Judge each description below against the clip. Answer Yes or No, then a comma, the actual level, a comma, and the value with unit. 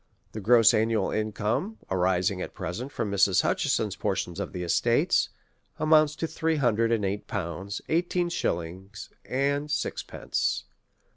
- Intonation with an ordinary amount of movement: No, wide, 6.8 semitones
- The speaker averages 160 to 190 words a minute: No, slow, 135 wpm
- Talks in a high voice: No, low, 110 Hz